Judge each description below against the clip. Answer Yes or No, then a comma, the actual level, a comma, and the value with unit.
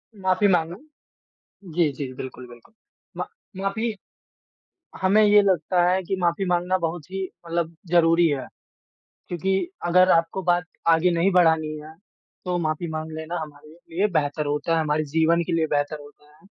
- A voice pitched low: No, medium, 170 Hz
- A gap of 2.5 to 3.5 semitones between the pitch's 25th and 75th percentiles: Yes, average, 2.8 semitones